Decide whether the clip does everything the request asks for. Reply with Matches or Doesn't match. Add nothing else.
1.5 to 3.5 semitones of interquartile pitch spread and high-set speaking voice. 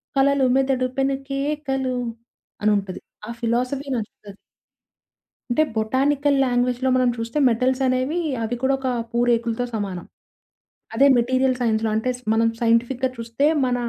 Matches